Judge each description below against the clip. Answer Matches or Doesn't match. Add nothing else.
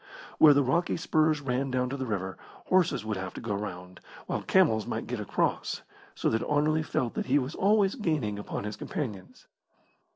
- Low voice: Matches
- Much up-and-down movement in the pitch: Matches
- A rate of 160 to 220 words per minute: Matches